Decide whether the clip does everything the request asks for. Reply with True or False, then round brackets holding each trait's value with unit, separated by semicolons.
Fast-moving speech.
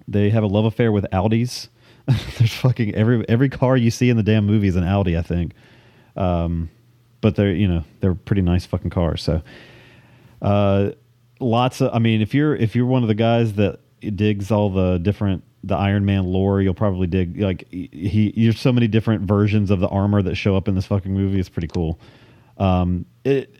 True (210 wpm)